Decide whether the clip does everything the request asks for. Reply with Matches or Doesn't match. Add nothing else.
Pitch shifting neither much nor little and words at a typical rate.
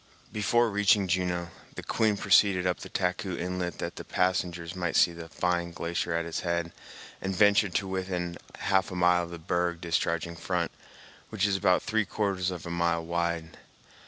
Doesn't match